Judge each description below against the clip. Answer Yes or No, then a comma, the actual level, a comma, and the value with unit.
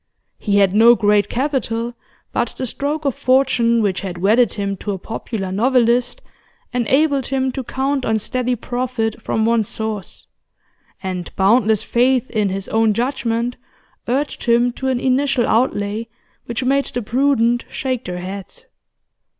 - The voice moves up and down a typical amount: Yes, average, 3.5 semitones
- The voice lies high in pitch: Yes, high, 235 Hz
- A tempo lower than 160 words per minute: Yes, average, 150 wpm